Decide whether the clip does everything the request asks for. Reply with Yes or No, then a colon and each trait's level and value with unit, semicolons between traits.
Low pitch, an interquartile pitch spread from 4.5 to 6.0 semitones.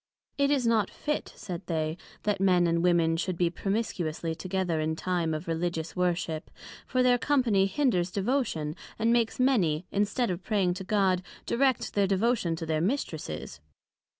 No: medium, 185 Hz; average, 5.2 semitones